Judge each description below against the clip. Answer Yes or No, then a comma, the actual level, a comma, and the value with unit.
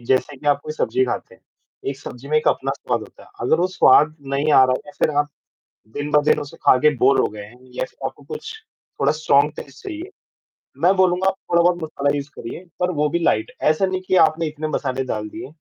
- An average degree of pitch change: Yes, average, 4.2 semitones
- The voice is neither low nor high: Yes, medium, 150 Hz